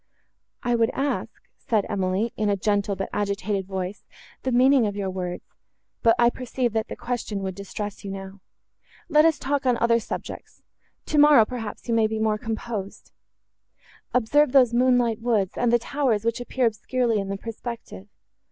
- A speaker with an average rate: Yes, average, 170 wpm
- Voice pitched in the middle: No, high, 225 Hz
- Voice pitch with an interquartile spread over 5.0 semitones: No, average, 3.5 semitones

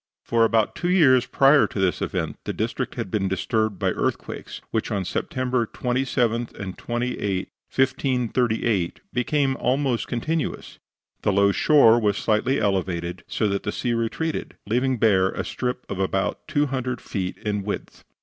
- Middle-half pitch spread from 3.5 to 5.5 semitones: Yes, average, 4.3 semitones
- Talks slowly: No, average, 150 wpm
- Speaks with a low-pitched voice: Yes, low, 115 Hz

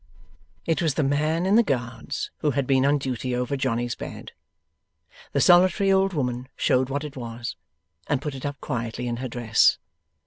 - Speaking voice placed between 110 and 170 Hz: Yes, low, 135 Hz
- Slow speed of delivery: No, average, 180 wpm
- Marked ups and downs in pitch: No, average, 3.7 semitones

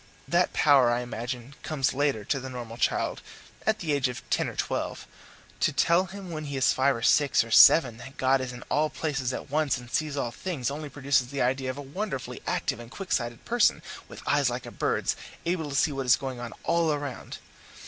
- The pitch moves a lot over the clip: No, average, 3.6 semitones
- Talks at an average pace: No, fast, 220 wpm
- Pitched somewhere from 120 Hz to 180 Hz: Yes, low, 135 Hz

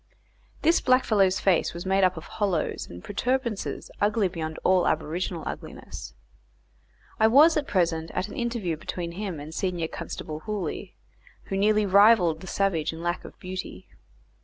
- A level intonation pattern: No, average, 4.1 semitones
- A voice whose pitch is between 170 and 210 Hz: Yes, medium, 185 Hz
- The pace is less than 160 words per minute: Yes, average, 150 wpm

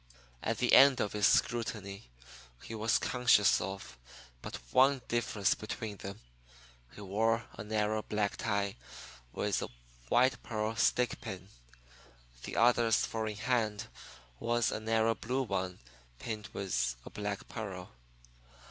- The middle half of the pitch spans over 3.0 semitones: No, narrow, 2.5 semitones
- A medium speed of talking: No, slow, 130 wpm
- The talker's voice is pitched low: Yes, low, 110 Hz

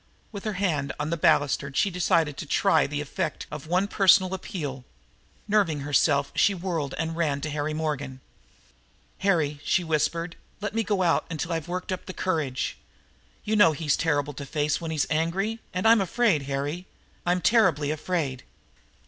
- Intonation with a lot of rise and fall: No, average, 4.2 semitones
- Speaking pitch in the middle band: Yes, medium, 165 Hz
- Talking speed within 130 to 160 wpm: No, average, 170 wpm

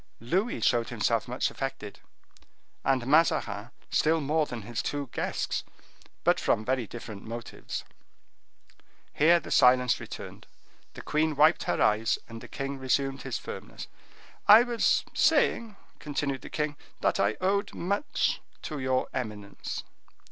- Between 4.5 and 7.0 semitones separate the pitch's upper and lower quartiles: Yes, average, 4.8 semitones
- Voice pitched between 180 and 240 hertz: No, low, 135 Hz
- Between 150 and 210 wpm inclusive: No, slow, 135 wpm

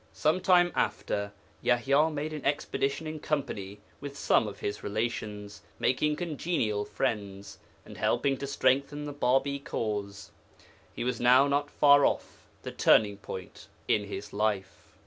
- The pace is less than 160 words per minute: Yes, average, 145 wpm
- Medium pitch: No, low, 130 Hz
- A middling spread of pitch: No, wide, 5.9 semitones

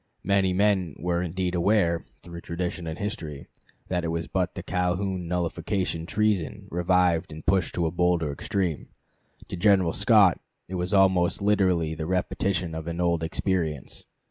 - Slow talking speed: No, average, 155 wpm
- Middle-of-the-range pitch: No, very low, 90 Hz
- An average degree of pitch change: No, narrow, 2.2 semitones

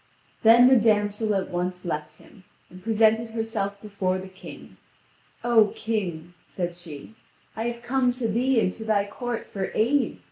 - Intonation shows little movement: No, average, 3.6 semitones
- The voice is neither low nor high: No, high, 215 Hz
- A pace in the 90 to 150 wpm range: No, average, 165 wpm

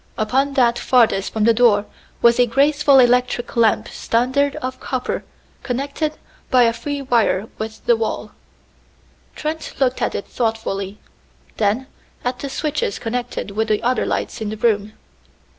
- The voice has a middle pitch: No, high, 240 Hz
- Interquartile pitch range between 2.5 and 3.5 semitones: Yes, average, 3.2 semitones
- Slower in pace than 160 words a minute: Yes, average, 150 wpm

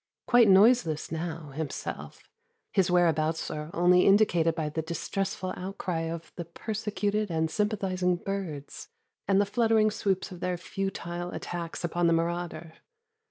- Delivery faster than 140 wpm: No, slow, 135 wpm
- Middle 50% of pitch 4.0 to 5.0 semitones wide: No, average, 3.1 semitones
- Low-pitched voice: No, medium, 175 Hz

